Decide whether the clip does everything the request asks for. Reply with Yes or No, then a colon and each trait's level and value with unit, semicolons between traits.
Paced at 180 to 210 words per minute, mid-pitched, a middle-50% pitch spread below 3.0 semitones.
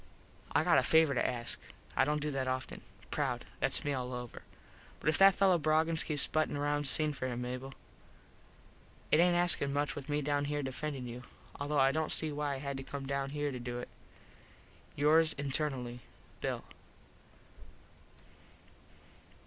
No: average, 170 wpm; medium, 145 Hz; narrow, 2.4 semitones